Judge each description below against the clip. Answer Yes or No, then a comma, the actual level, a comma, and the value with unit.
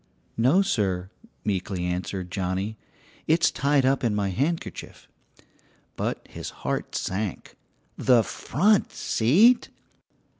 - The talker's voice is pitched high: No, low, 110 Hz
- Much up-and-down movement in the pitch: Yes, wide, 7.4 semitones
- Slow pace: Yes, slow, 105 wpm